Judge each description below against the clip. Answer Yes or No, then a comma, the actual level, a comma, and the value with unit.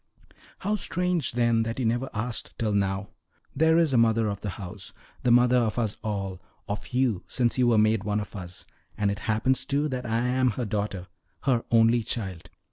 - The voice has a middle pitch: No, low, 115 Hz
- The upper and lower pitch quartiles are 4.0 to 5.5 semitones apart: No, average, 3.4 semitones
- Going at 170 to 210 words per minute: Yes, average, 200 wpm